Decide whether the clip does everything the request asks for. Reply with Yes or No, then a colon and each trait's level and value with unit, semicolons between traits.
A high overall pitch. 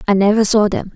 Yes: high, 205 Hz